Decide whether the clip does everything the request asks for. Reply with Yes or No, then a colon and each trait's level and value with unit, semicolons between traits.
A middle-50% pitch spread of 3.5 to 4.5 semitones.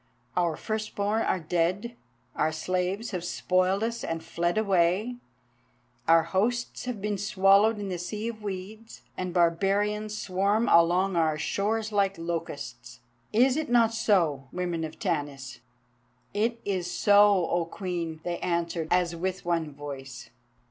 Yes: average, 3.9 semitones